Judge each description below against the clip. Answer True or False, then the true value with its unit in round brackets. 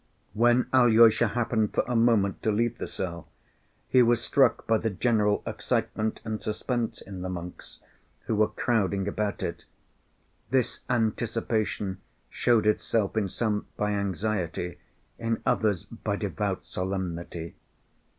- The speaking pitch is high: False (110 Hz)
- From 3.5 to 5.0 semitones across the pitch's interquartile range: False (2.9 semitones)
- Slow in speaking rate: True (130 wpm)